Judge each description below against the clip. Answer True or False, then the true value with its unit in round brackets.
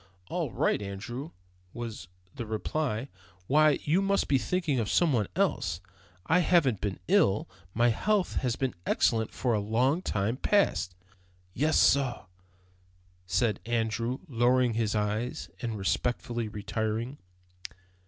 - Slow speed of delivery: True (130 wpm)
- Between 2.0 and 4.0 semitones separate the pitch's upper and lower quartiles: False (4.6 semitones)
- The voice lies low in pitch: True (120 Hz)